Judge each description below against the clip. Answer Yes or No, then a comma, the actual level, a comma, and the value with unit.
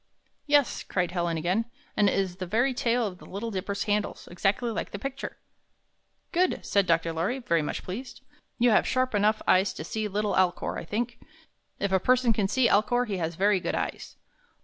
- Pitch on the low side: No, high, 205 Hz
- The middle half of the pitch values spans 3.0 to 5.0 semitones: Yes, average, 4.5 semitones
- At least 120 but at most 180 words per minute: No, average, 195 wpm